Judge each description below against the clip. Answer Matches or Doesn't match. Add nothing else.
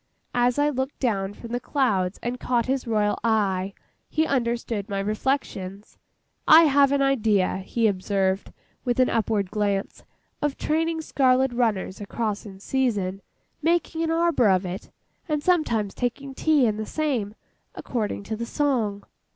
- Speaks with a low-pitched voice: Doesn't match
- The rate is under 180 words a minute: Matches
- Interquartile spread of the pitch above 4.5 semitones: Matches